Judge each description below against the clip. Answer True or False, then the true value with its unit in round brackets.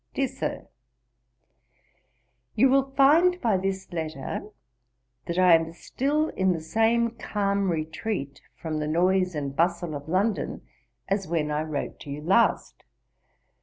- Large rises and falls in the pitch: True (6.0 semitones)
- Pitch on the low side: False (185 Hz)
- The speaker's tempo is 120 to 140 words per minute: True (135 wpm)